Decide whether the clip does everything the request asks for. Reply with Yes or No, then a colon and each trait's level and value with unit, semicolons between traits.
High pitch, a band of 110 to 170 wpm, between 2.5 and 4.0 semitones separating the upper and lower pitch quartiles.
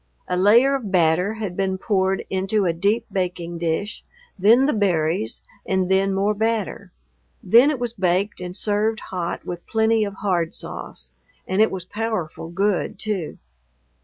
Yes: high, 195 Hz; average, 160 wpm; average, 3.2 semitones